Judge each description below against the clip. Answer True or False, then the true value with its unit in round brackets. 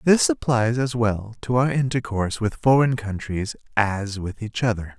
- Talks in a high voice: False (115 Hz)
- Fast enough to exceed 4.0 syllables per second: True (4.5 syllables/s)